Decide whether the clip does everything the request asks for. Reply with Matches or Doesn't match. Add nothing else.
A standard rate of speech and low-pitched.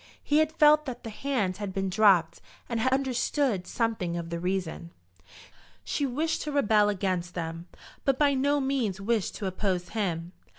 Doesn't match